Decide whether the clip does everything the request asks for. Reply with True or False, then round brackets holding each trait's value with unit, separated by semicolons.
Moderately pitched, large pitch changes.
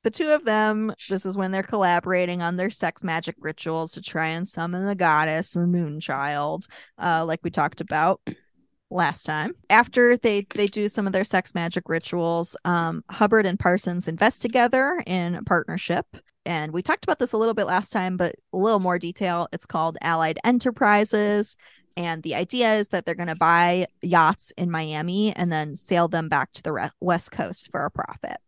False (180 Hz; 3.8 semitones)